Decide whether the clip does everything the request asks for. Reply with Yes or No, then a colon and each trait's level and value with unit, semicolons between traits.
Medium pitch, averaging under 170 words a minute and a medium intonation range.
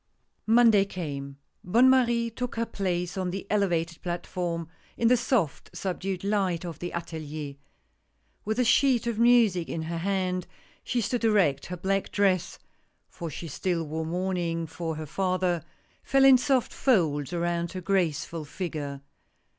Yes: medium, 180 Hz; average, 160 wpm; average, 4.2 semitones